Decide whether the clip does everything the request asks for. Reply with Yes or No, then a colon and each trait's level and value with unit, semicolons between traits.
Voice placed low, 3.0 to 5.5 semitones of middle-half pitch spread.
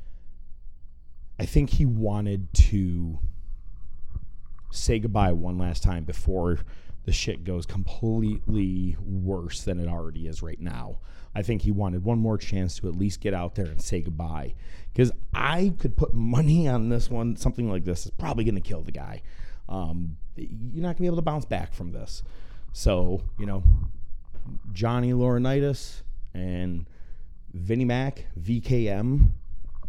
Yes: very low, 95 Hz; average, 5.1 semitones